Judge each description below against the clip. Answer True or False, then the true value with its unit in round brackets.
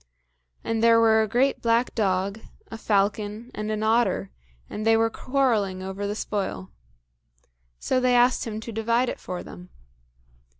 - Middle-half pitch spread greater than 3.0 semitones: False (2.4 semitones)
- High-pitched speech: True (220 Hz)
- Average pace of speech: True (160 wpm)